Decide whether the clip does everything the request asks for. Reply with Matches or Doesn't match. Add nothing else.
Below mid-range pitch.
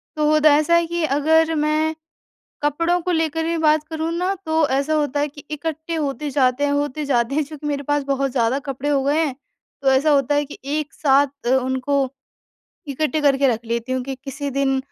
Doesn't match